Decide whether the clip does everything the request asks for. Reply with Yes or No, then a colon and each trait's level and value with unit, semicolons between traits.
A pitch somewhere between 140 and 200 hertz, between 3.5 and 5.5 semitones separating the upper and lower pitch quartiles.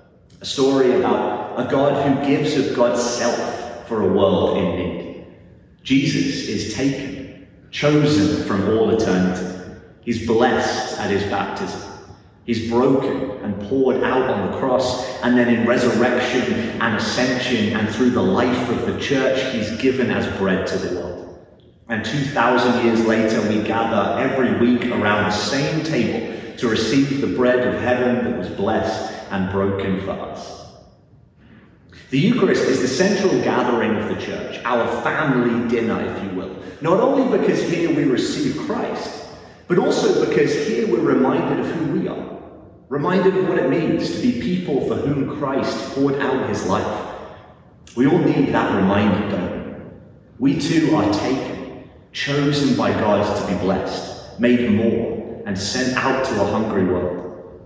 No: low, 120 Hz; average, 4.5 semitones